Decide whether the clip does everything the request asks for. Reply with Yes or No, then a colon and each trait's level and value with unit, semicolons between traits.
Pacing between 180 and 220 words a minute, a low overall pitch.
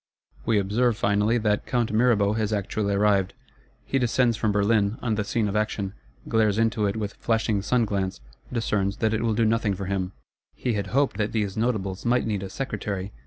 Yes: average, 190 wpm; low, 105 Hz